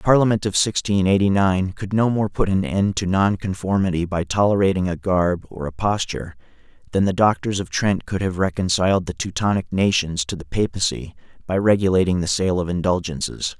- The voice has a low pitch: Yes, very low, 95 Hz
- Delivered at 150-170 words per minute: No, average, 180 wpm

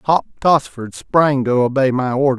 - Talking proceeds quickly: No, average, 175 wpm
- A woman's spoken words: No, male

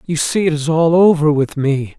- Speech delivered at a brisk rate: Yes, fast, 240 wpm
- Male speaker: Yes, male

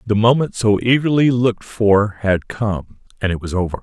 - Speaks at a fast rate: No, average, 190 wpm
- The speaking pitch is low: Yes, low, 105 Hz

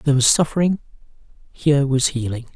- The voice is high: No, medium, 140 Hz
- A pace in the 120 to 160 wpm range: Yes, average, 140 wpm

